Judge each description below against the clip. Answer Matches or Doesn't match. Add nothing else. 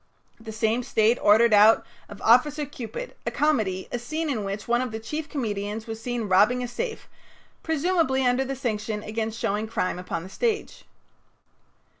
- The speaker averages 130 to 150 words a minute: Doesn't match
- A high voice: Matches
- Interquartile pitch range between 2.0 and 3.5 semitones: Doesn't match